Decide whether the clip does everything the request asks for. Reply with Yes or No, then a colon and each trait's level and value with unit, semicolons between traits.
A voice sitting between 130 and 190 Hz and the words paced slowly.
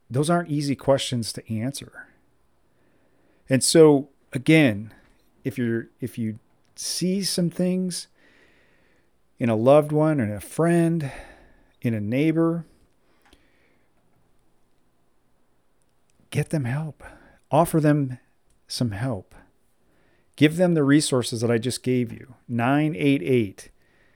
Yes: low, 135 Hz; slow, 110 wpm